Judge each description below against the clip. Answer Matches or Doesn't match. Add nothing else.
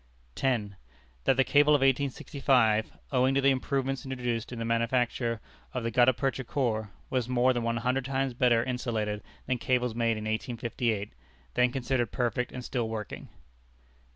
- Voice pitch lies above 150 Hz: Doesn't match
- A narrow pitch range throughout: Matches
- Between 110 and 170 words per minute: Matches